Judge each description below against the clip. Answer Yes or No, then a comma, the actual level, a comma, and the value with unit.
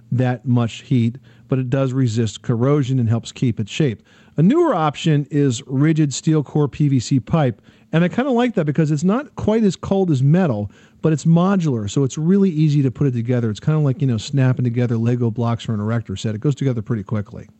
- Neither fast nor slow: No, fast, 225 wpm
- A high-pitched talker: No, low, 135 Hz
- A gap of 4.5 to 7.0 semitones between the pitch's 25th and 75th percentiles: Yes, average, 4.8 semitones